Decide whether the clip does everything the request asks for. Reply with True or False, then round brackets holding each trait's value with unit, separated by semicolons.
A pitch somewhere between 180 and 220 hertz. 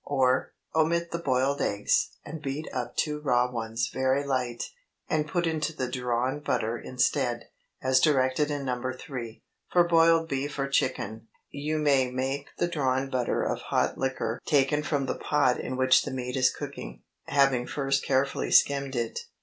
False (135 Hz)